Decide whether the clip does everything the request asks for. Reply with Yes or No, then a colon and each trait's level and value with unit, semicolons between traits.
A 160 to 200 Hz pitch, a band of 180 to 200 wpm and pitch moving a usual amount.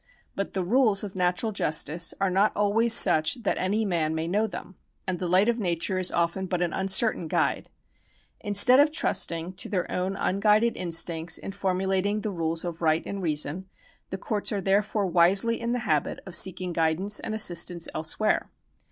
Yes: high, 190 Hz; average, 185 wpm; average, 3.3 semitones